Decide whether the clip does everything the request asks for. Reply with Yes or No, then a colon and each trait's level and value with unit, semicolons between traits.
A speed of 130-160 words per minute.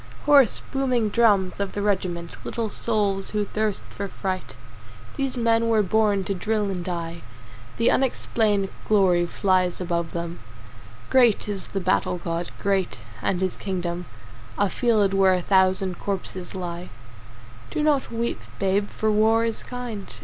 Yes: average, 150 wpm